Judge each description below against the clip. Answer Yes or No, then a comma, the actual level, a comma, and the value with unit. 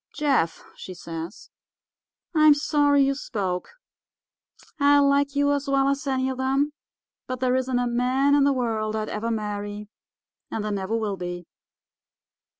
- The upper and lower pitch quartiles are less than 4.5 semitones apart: No, average, 5.0 semitones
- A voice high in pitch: Yes, very high, 255 Hz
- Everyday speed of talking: Yes, average, 150 wpm